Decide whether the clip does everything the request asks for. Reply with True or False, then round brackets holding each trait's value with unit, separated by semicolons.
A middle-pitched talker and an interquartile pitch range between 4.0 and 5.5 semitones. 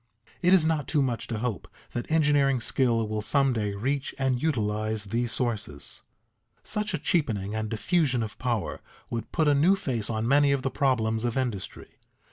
False (125 Hz; 4.5 semitones)